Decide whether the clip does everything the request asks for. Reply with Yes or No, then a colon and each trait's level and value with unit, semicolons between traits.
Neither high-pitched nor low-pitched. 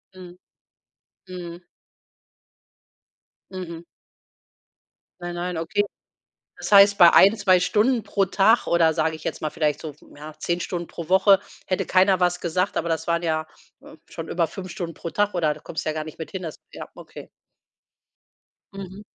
Yes: medium, 175 Hz